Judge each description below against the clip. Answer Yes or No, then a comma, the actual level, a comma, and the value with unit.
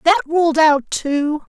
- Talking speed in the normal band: Yes, average, 150 wpm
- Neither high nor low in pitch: No, very high, 305 Hz